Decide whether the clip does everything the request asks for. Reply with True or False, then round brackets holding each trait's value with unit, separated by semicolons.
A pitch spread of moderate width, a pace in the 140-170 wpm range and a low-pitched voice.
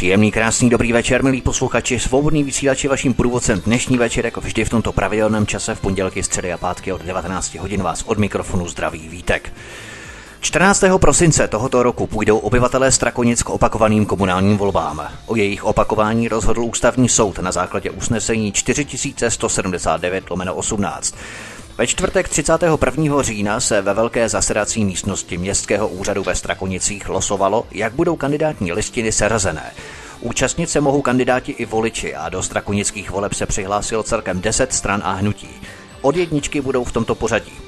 True (4.4 semitones; 150 wpm; 110 Hz)